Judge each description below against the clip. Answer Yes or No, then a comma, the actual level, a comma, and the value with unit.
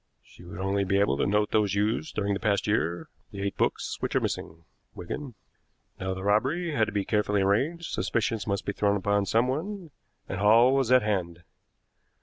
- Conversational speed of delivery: Yes, average, 190 wpm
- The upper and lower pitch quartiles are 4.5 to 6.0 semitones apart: No, average, 3.3 semitones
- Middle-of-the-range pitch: No, low, 105 Hz